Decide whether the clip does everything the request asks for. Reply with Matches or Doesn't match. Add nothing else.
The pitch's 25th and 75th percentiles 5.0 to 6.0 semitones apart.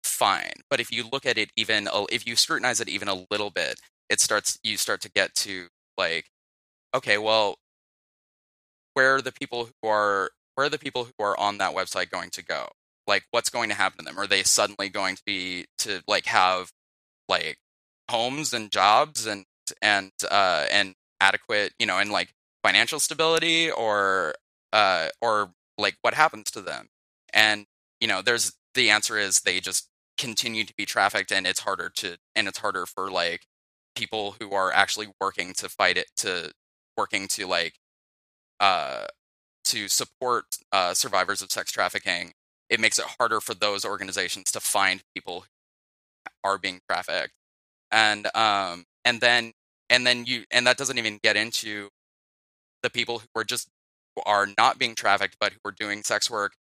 Doesn't match